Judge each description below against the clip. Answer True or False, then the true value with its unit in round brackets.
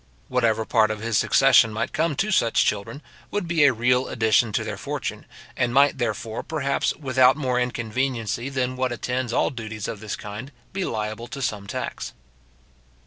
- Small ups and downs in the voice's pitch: False (3.3 semitones)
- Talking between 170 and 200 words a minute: True (175 wpm)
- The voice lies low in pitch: True (125 Hz)